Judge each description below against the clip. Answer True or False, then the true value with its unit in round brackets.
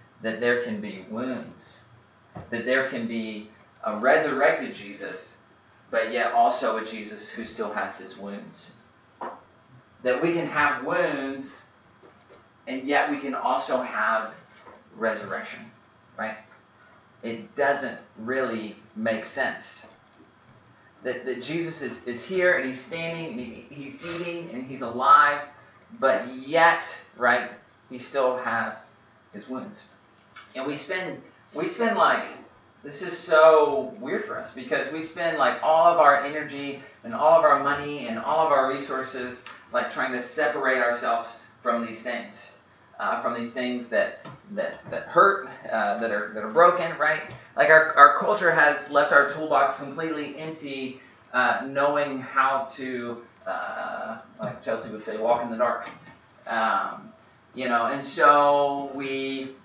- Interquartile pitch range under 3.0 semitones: False (3.7 semitones)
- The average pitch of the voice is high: False (135 Hz)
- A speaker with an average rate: True (145 wpm)